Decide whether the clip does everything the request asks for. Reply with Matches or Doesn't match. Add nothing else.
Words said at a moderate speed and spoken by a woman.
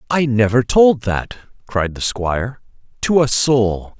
Doesn't match